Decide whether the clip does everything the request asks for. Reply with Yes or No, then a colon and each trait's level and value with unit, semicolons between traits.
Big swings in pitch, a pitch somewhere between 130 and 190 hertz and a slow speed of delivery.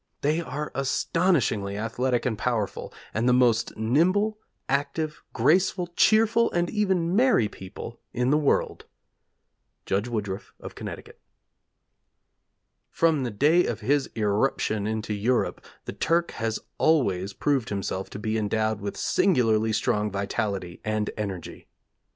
No: wide, 6.9 semitones; low, 120 Hz; slow, 125 wpm